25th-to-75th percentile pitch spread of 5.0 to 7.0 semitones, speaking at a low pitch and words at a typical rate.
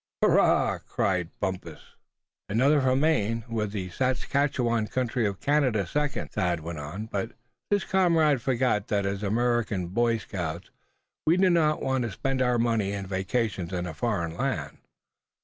Yes: wide, 5.4 semitones; low, 115 Hz; average, 150 wpm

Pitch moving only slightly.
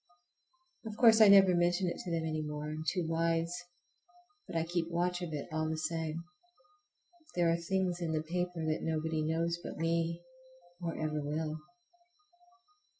Yes: narrow, 2.0 semitones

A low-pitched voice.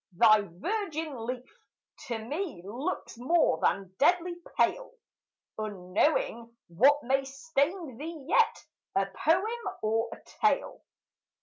No: very high, 270 Hz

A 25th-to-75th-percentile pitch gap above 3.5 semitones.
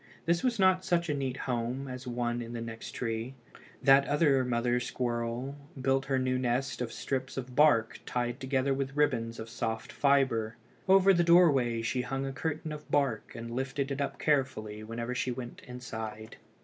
No: average, 2.9 semitones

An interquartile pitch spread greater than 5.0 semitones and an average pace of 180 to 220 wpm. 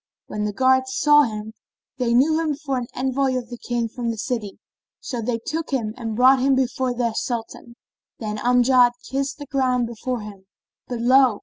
No: narrow, 2.4 semitones; average, 190 wpm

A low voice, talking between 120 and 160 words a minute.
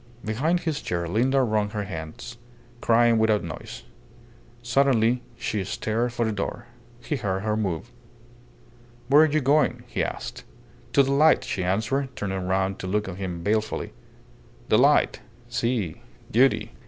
Yes: low, 110 Hz; average, 150 wpm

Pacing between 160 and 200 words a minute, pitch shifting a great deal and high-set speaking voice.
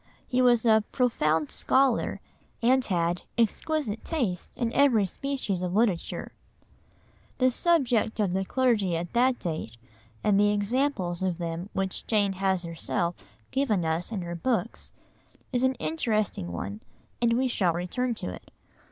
No: average, 145 wpm; wide, 6.1 semitones; high, 210 Hz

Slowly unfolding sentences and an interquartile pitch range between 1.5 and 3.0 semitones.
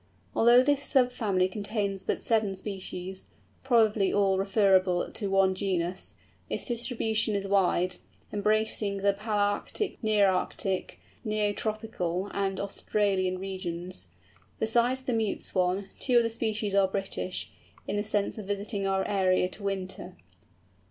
Yes: slow, 130 wpm; narrow, 2.4 semitones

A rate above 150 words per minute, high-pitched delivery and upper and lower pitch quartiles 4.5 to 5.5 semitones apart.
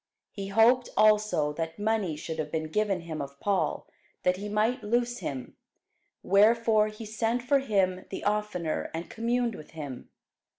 Yes: average, 160 wpm; high, 210 Hz; average, 5.2 semitones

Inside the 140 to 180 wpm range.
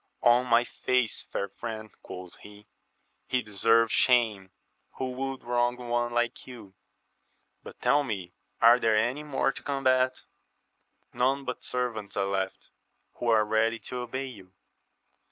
Yes: average, 145 wpm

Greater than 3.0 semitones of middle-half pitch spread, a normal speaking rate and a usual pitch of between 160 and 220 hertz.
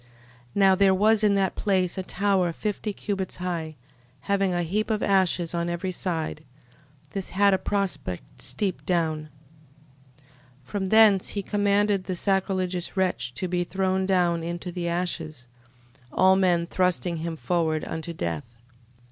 No: narrow, 2.5 semitones; average, 150 wpm; medium, 185 Hz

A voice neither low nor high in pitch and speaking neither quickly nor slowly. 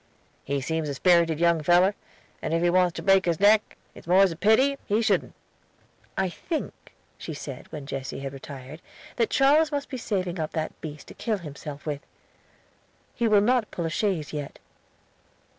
Yes: medium, 175 Hz; average, 180 wpm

